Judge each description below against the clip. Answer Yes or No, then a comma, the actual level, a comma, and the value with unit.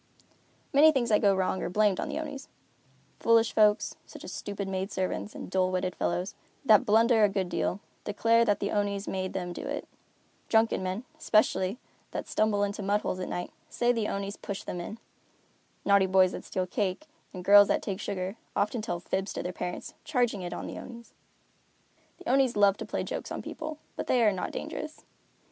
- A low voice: No, high, 205 Hz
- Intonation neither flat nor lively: Yes, average, 3.3 semitones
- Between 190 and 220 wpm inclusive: Yes, average, 200 wpm